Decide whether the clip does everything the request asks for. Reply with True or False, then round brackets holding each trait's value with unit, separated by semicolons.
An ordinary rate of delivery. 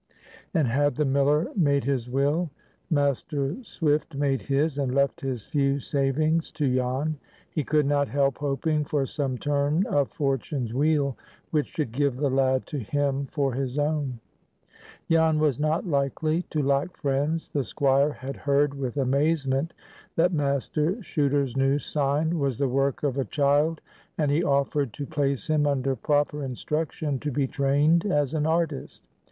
True (160 wpm)